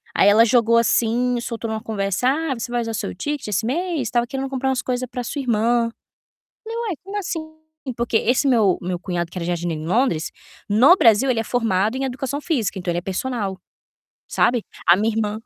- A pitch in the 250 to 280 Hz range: No, high, 235 Hz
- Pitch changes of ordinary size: Yes, average, 4.2 semitones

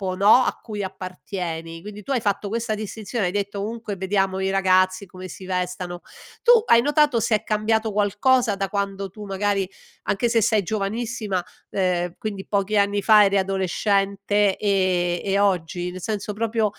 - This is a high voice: Yes, high, 200 Hz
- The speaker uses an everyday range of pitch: No, narrow, 2.2 semitones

